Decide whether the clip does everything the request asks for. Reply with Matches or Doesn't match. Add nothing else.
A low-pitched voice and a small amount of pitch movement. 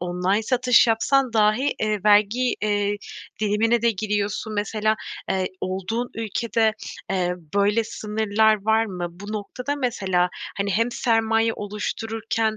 Doesn't match